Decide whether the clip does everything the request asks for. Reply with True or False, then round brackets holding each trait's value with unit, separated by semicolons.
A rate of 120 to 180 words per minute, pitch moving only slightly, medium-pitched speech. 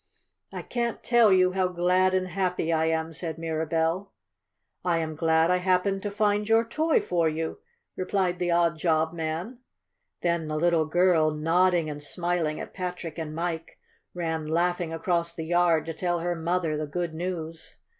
True (170 wpm; 2.1 semitones; 170 Hz)